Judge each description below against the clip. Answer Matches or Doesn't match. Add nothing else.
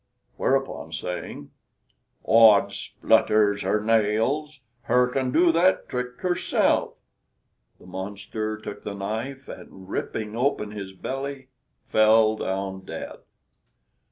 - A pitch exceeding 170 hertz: Doesn't match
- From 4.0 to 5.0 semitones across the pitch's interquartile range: Matches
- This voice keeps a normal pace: Doesn't match